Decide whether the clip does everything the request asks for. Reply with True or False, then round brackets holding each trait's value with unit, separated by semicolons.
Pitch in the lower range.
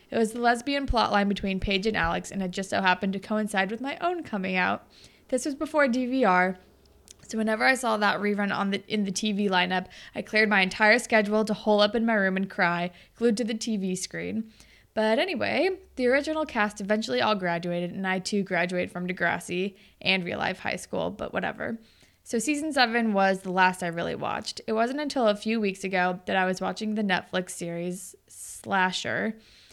False (205 Hz)